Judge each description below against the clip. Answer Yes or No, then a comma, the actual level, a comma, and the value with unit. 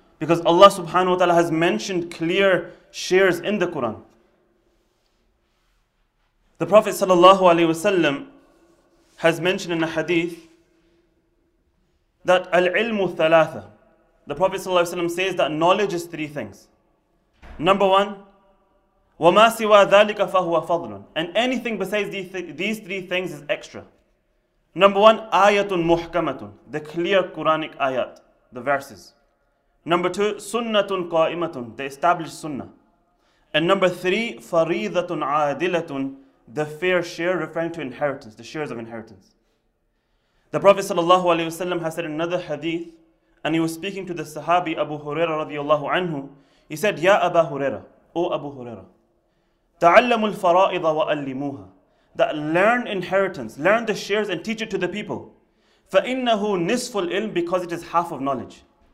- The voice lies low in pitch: No, medium, 175 Hz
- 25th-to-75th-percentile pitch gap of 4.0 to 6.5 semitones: No, average, 3.6 semitones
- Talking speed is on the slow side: Yes, slow, 125 wpm